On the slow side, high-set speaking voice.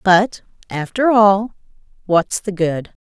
Yes: slow, 120 wpm; high, 195 Hz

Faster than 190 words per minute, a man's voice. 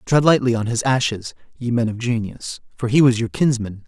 Yes: average, 200 wpm; male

